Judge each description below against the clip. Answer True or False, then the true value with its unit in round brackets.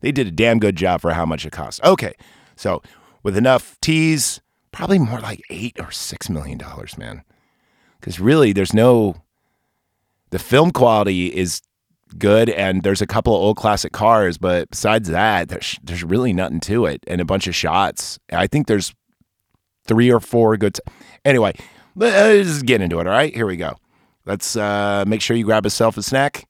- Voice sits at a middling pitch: False (105 Hz)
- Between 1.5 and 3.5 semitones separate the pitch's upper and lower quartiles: False (4.2 semitones)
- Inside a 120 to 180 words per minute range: False (190 wpm)